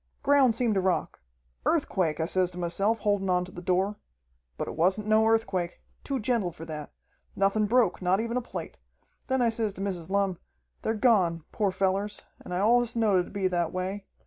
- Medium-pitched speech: No, high, 195 Hz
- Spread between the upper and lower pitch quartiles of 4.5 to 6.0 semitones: No, average, 3.6 semitones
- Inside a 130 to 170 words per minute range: No, average, 200 wpm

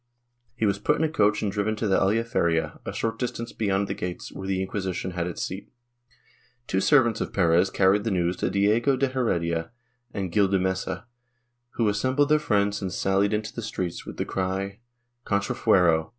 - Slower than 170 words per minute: No, average, 190 wpm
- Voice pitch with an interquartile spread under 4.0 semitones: Yes, average, 3.2 semitones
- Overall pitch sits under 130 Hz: Yes, low, 100 Hz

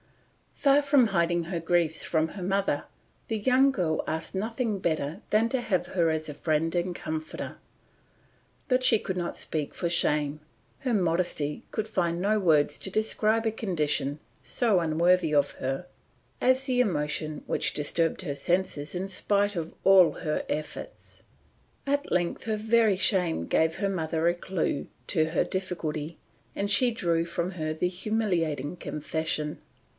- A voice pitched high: No, medium, 175 Hz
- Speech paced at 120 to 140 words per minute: No, average, 155 wpm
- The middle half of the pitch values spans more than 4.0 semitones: Yes, average, 4.7 semitones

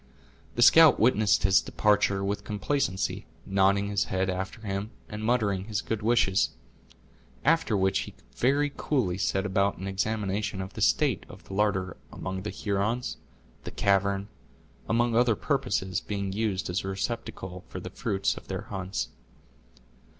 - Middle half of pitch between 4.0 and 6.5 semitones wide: No, narrow, 2.6 semitones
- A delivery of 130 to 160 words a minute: Yes, average, 150 wpm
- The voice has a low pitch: Yes, low, 100 Hz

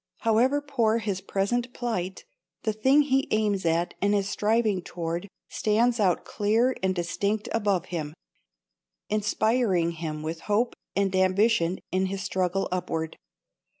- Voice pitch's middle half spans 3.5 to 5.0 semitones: Yes, average, 3.8 semitones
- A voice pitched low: No, high, 200 Hz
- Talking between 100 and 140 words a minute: Yes, slow, 135 wpm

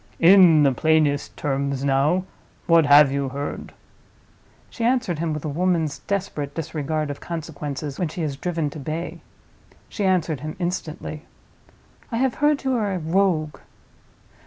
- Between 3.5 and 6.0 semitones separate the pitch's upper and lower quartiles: Yes, average, 3.9 semitones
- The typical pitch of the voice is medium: Yes, medium, 155 Hz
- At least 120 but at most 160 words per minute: Yes, average, 145 wpm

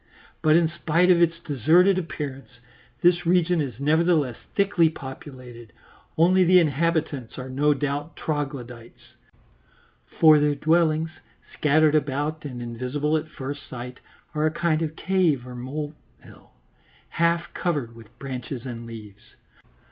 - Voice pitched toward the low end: No, medium, 150 Hz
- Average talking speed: No, slow, 130 wpm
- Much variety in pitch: No, average, 4.3 semitones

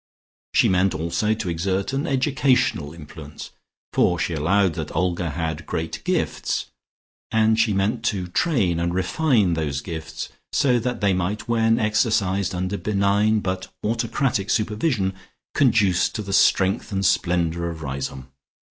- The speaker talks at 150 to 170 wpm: No, average, 140 wpm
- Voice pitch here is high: No, very low, 95 Hz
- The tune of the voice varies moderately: Yes, average, 4.5 semitones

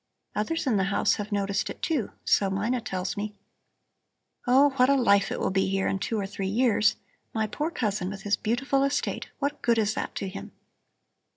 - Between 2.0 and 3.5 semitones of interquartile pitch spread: No, average, 4.2 semitones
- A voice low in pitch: No, high, 210 Hz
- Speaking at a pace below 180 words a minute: No, average, 200 wpm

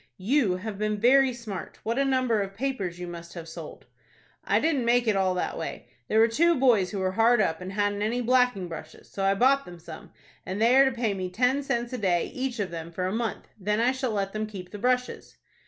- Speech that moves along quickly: Yes, fast, 240 wpm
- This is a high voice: Yes, high, 215 Hz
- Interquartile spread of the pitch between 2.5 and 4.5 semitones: No, average, 4.9 semitones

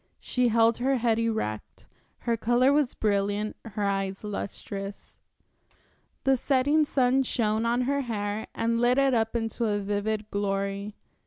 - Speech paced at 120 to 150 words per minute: Yes, average, 145 wpm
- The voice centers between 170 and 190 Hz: No, high, 225 Hz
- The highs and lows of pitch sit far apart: No, average, 3.3 semitones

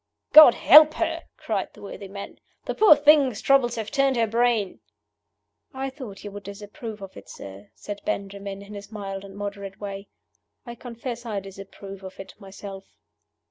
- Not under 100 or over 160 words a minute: No, average, 170 wpm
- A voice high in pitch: Yes, high, 205 Hz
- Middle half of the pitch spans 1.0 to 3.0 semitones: No, average, 3.5 semitones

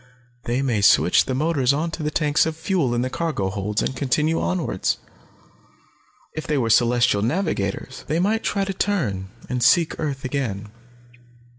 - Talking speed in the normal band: Yes, average, 160 wpm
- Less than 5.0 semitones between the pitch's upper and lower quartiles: No, wide, 5.6 semitones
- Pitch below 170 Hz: Yes, low, 135 Hz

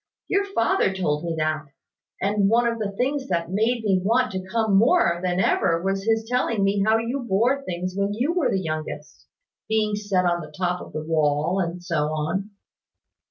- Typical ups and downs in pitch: Yes, average, 4.6 semitones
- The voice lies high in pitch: Yes, high, 195 Hz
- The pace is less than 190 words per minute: No, average, 195 wpm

